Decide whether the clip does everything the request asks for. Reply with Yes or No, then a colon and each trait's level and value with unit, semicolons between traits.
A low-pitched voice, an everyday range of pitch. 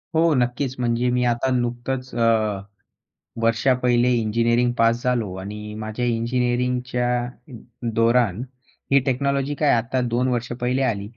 No: low, 120 Hz; narrow, 1.6 semitones